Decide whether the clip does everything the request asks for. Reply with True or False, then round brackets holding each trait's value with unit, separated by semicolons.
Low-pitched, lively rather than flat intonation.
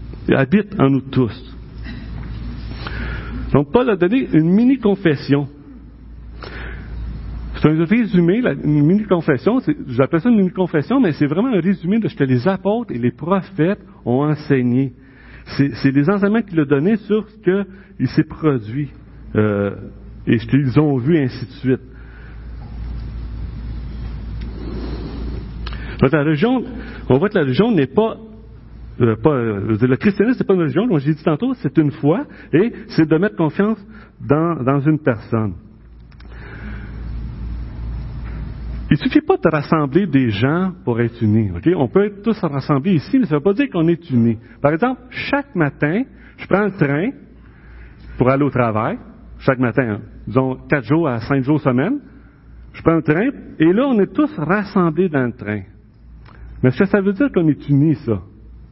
False (150 Hz; 7.1 semitones)